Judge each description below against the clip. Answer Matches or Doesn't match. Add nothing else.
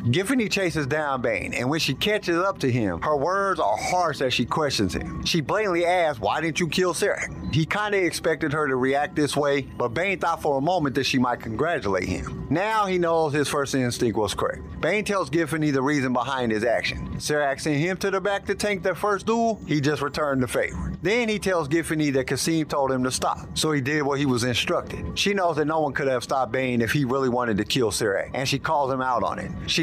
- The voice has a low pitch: Doesn't match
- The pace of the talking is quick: Matches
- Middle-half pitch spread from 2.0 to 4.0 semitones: Doesn't match